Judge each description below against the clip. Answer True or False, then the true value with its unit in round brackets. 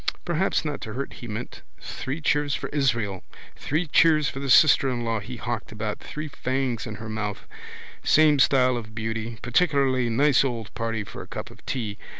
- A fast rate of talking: False (185 wpm)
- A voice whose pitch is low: True (125 Hz)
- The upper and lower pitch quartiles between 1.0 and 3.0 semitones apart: False (4.1 semitones)